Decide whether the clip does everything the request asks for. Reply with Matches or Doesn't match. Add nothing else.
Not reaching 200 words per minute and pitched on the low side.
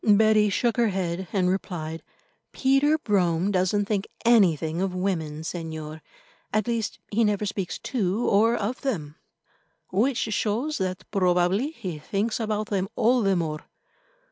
Doesn't match